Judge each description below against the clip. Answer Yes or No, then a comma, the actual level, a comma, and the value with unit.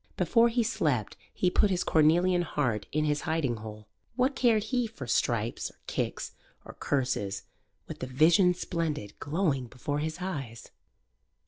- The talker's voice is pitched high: No, medium, 155 Hz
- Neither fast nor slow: Yes, average, 150 wpm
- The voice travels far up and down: Yes, wide, 6.6 semitones